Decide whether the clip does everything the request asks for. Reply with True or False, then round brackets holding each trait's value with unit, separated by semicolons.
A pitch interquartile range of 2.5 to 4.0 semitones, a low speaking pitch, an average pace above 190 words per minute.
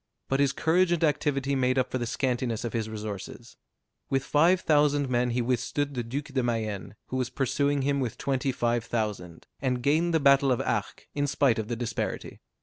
True (3.1 semitones; 130 Hz; 200 wpm)